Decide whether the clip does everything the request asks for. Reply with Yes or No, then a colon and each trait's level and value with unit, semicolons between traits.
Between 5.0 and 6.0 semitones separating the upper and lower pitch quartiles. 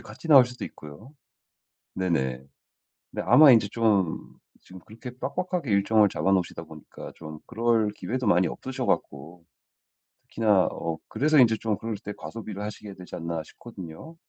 Yes: wide, 5.6 semitones